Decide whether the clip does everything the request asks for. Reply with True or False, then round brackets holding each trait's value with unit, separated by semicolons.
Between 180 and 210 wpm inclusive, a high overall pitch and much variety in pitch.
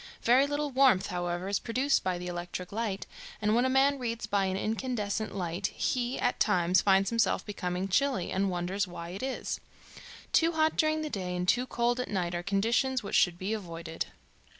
True (195 wpm; 205 Hz; 5.7 semitones)